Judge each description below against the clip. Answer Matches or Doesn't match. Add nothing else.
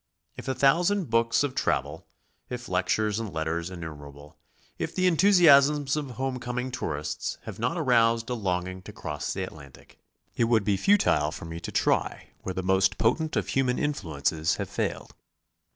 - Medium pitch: Doesn't match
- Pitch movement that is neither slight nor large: Doesn't match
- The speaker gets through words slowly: Doesn't match